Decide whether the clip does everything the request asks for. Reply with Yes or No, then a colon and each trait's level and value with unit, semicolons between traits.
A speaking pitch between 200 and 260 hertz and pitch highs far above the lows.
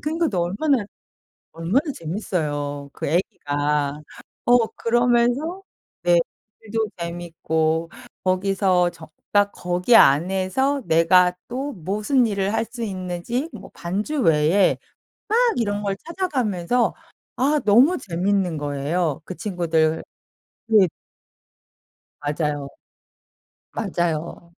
No: medium, 185 Hz; wide, 5.8 semitones